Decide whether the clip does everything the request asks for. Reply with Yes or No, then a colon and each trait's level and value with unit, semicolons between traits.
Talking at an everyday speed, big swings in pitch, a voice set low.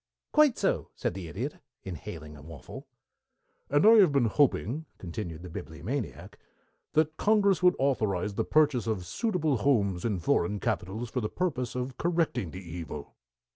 Yes: average, 155 wpm; wide, 9.0 semitones; low, 120 Hz